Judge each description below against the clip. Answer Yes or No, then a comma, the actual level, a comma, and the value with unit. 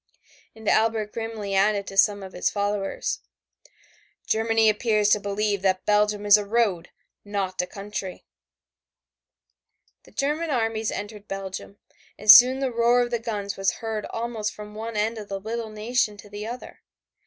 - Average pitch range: No, narrow, 1.9 semitones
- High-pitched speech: Yes, high, 210 Hz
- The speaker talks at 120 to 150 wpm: No, average, 160 wpm